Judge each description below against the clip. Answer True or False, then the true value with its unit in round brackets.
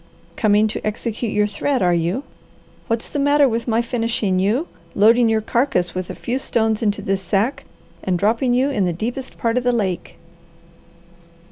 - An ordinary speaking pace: True (175 wpm)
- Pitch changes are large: False (3.3 semitones)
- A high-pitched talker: True (225 Hz)